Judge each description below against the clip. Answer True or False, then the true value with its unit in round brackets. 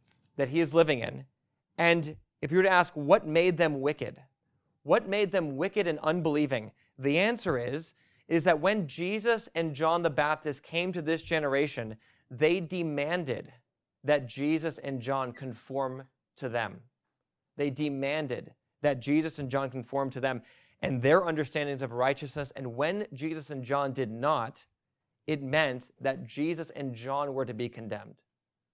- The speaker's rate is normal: True (160 wpm)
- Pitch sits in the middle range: True (145 Hz)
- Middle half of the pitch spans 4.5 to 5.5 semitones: False (3.5 semitones)